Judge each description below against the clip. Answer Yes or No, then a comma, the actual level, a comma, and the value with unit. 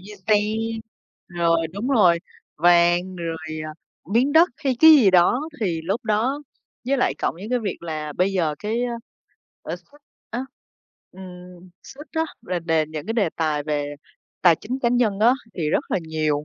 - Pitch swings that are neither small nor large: No, wide, 6.4 semitones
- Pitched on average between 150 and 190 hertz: Yes, medium, 185 Hz